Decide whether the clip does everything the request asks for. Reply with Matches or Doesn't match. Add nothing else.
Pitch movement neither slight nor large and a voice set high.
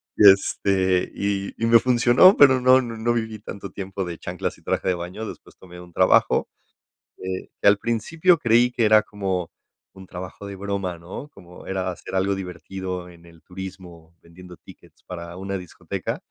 Doesn't match